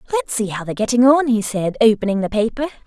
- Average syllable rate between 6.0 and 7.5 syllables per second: Yes, 6.6 syllables/s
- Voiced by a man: No, female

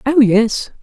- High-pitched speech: Yes, high, 245 Hz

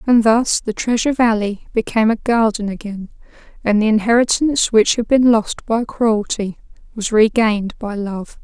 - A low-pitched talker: No, high, 220 Hz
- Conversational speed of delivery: Yes, average, 155 wpm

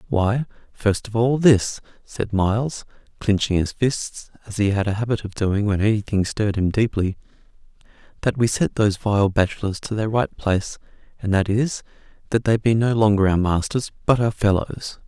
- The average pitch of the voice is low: Yes, low, 105 Hz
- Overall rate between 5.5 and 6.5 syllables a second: No, 5.0 syllables/s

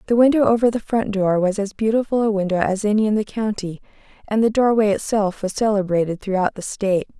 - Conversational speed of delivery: No, fast, 210 wpm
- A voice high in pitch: Yes, high, 210 Hz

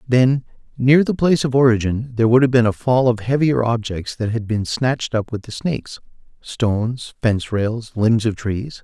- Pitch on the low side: Yes, low, 120 Hz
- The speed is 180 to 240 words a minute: Yes, average, 190 wpm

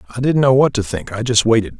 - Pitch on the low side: Yes, low, 120 Hz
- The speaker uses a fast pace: Yes, fast, 300 wpm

